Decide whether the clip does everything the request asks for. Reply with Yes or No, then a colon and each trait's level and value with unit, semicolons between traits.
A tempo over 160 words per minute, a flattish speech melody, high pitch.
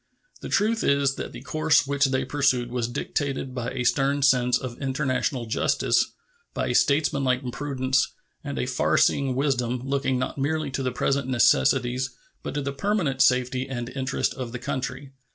No: average, 170 wpm; narrow, 1.8 semitones; low, 130 Hz